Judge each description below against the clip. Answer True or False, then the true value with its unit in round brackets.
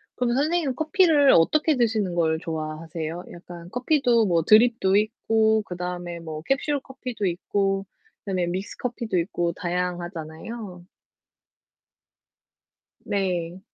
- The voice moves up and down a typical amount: False (5.7 semitones)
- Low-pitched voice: False (195 Hz)